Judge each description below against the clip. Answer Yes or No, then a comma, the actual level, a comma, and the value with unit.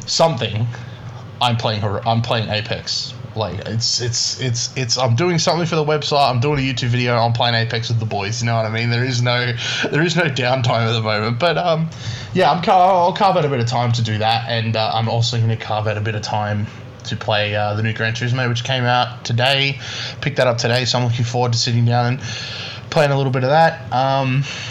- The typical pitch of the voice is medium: No, low, 120 Hz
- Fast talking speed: Yes, fast, 245 wpm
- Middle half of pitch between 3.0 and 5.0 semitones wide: No, narrow, 2.4 semitones